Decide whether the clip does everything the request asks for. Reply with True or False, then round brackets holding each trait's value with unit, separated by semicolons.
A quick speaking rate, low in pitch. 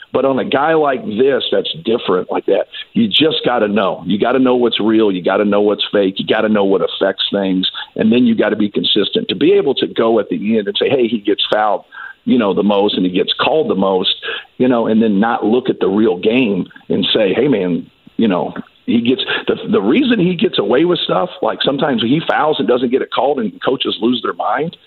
True (240 wpm; 130 Hz)